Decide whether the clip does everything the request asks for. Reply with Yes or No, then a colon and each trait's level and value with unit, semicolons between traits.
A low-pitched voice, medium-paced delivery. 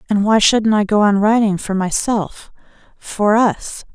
No: high, 210 Hz; average, 150 wpm